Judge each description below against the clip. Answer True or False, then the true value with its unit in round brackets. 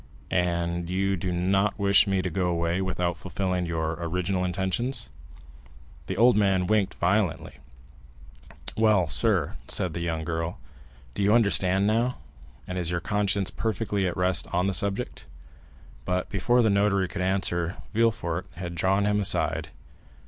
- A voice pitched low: True (95 Hz)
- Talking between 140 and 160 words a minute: True (150 wpm)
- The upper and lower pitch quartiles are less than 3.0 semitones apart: True (2.5 semitones)